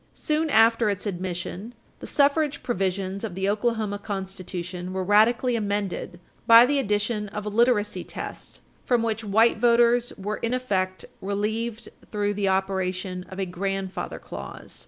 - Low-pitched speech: No, high, 205 Hz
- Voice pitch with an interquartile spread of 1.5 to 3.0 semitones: No, average, 3.4 semitones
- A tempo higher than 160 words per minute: No, average, 145 wpm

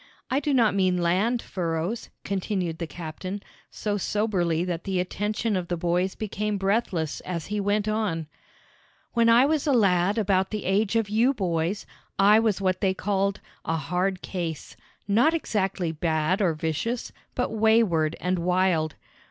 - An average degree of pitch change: Yes, average, 3.6 semitones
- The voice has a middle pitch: No, high, 195 Hz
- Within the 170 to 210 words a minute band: No, average, 160 wpm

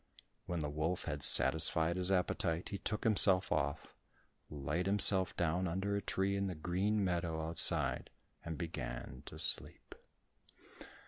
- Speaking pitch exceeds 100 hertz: No, very low, 90 Hz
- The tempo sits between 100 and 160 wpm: Yes, average, 140 wpm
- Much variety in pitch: No, average, 3.2 semitones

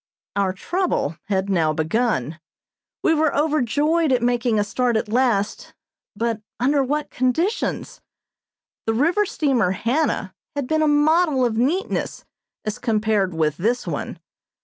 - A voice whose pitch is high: Yes, high, 245 Hz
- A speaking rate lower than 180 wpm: Yes, slow, 135 wpm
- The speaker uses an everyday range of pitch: No, wide, 6.3 semitones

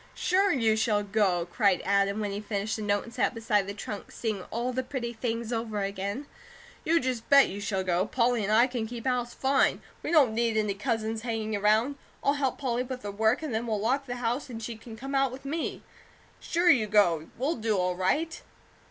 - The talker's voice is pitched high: Yes, high, 225 Hz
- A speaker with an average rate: No, fast, 220 wpm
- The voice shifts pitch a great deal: No, average, 3.6 semitones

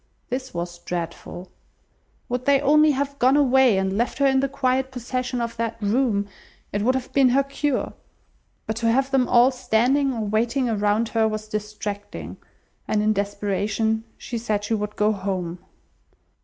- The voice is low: No, high, 230 Hz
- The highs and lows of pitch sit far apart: No, average, 3.9 semitones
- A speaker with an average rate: Yes, average, 170 wpm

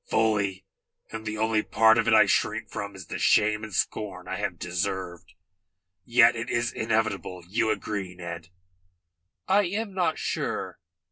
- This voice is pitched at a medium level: No, low, 110 Hz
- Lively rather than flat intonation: No, average, 3.1 semitones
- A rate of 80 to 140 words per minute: No, average, 155 wpm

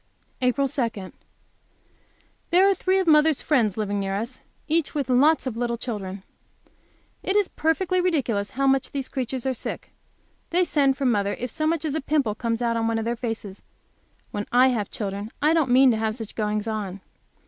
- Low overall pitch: No, very high, 250 Hz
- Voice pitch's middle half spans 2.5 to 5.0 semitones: No, wide, 5.6 semitones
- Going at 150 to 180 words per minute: No, average, 190 wpm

